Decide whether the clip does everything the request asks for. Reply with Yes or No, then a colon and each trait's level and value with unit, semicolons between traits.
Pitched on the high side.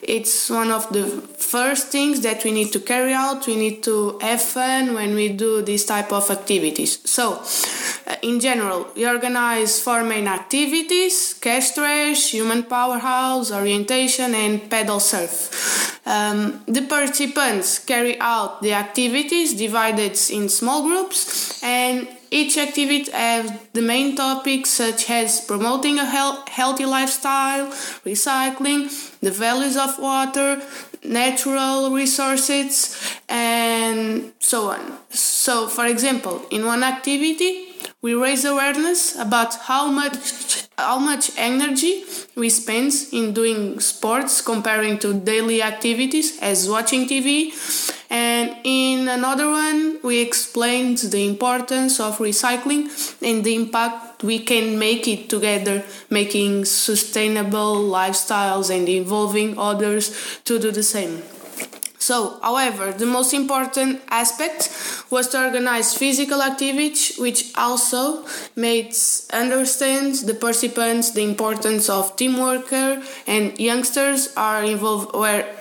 Yes: high, 240 Hz